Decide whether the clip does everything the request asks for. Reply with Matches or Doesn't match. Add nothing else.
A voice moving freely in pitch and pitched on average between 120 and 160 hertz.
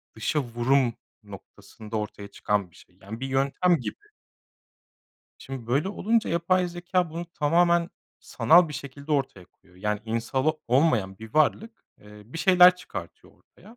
Matches